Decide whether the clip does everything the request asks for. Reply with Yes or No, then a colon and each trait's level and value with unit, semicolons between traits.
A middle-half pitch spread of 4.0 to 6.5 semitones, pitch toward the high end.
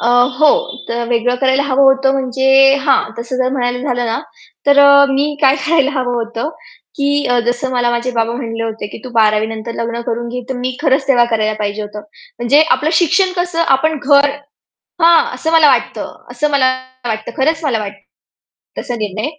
No: average, 3.4 semitones; very high, 255 Hz